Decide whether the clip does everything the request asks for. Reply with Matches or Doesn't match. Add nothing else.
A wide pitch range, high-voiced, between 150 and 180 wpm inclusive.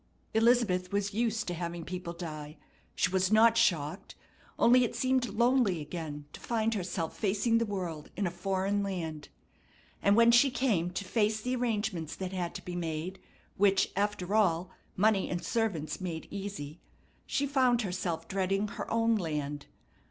Doesn't match